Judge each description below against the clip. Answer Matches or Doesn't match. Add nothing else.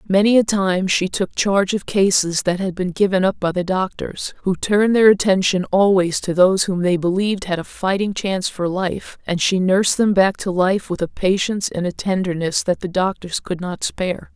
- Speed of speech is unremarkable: Doesn't match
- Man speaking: Doesn't match